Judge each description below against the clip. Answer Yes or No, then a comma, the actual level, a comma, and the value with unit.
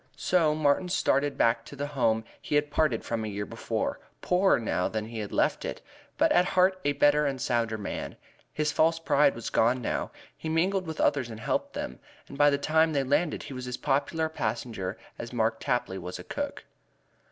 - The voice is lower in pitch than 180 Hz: Yes, medium, 140 Hz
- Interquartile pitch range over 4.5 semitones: Yes, average, 5.3 semitones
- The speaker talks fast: Yes, fast, 210 wpm